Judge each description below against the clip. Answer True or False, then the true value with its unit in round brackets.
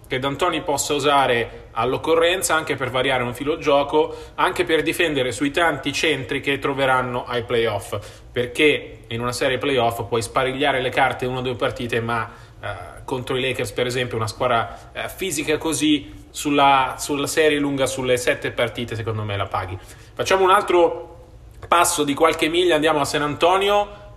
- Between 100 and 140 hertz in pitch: True (135 Hz)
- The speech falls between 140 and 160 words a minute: False (170 wpm)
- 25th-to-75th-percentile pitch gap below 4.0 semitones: False (4.4 semitones)